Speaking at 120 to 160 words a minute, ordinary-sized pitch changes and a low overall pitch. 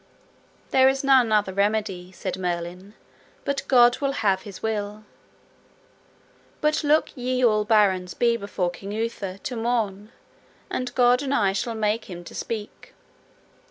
No: average, 145 wpm; average, 4.0 semitones; high, 215 Hz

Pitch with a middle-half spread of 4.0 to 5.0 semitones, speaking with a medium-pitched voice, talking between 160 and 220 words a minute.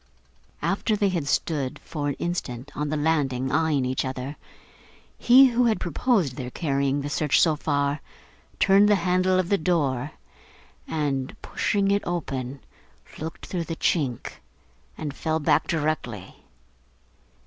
No: average, 4.6 semitones; medium, 155 Hz; average, 140 wpm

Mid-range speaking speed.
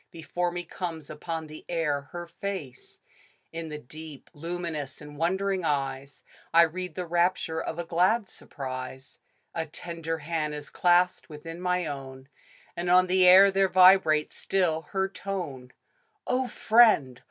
Yes: average, 145 wpm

